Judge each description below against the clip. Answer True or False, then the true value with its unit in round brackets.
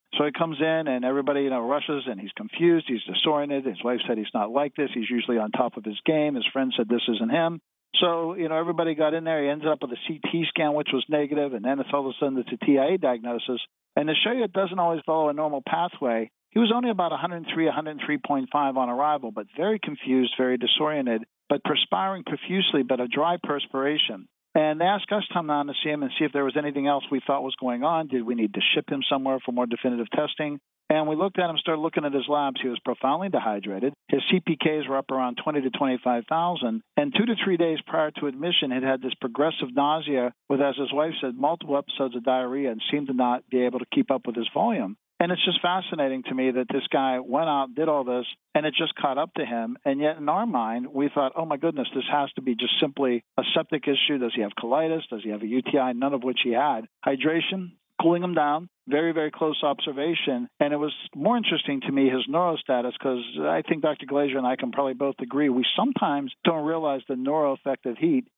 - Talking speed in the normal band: False (240 wpm)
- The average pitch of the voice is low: False (145 Hz)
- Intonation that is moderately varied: True (3.7 semitones)